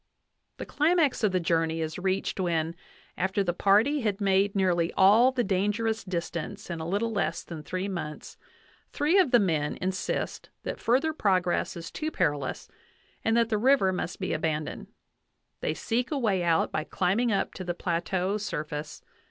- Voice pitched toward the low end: No, high, 190 Hz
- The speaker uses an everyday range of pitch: Yes, average, 4.8 semitones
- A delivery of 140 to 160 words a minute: No, average, 170 wpm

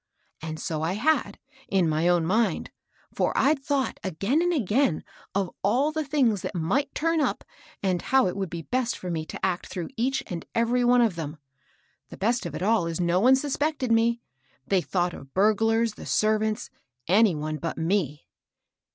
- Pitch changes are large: Yes, wide, 6.3 semitones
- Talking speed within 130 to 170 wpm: No, average, 185 wpm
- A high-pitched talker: Yes, high, 210 Hz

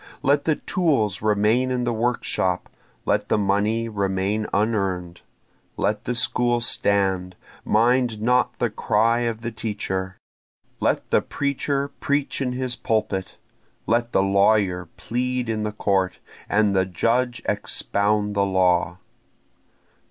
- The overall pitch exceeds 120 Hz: No, low, 110 Hz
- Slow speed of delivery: Yes, slow, 130 wpm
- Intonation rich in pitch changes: No, average, 3.6 semitones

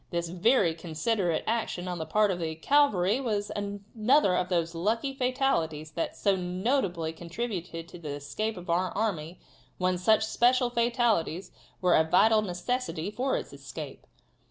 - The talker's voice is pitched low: No, medium, 185 Hz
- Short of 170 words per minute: Yes, average, 155 wpm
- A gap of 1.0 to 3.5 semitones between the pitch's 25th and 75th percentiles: No, average, 5.1 semitones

